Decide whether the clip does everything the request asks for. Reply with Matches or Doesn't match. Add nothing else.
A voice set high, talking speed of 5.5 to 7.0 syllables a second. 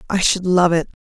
Doesn't match